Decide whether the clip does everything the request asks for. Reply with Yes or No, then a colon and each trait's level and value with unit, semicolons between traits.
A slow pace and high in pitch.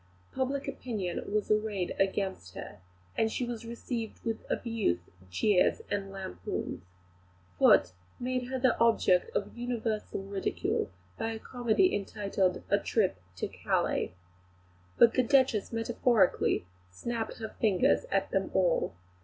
Yes: slow, 125 wpm; high, 220 Hz